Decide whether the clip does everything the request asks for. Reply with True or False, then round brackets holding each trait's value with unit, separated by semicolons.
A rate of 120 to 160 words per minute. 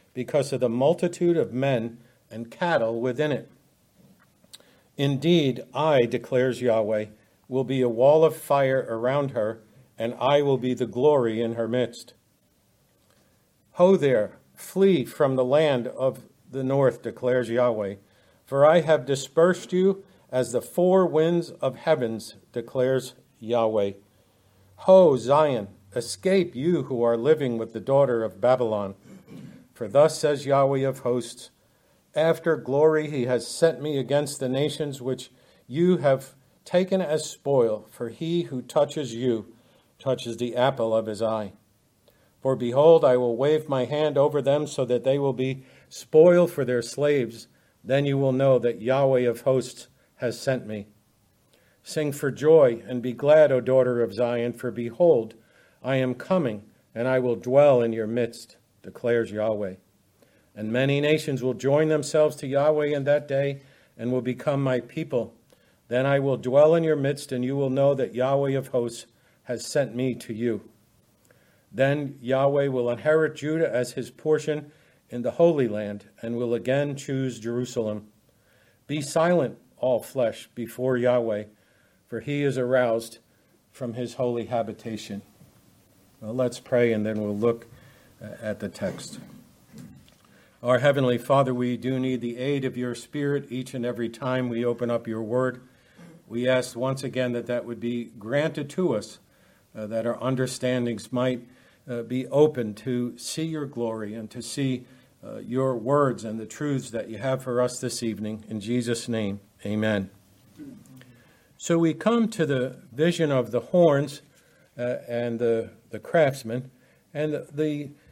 True (155 wpm)